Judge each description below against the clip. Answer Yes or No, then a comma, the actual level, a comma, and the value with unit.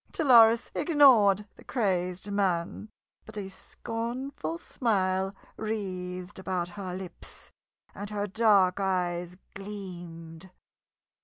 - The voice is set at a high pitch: Yes, high, 195 Hz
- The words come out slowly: Yes, slow, 95 wpm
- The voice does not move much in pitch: No, average, 3.2 semitones